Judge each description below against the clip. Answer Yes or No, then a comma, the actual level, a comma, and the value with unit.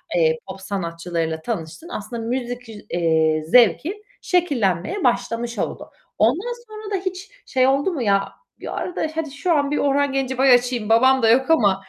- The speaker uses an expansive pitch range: Yes, wide, 6.7 semitones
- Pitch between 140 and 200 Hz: No, high, 245 Hz